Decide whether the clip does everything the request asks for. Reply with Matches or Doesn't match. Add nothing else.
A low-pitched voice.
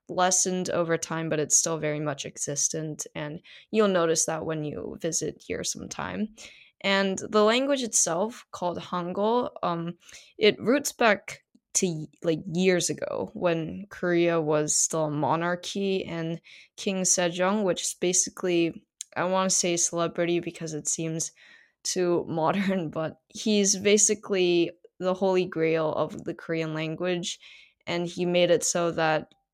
Doesn't match